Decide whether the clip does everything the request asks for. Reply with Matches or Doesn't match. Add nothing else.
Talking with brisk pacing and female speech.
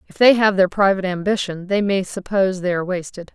Matches